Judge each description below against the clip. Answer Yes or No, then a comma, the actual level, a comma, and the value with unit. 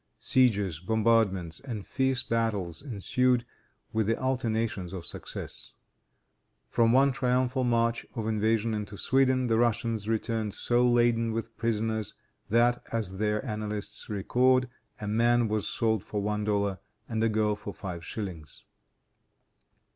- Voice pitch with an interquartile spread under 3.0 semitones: Yes, narrow, 2.4 semitones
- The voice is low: Yes, low, 110 Hz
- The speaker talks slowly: Yes, slow, 130 wpm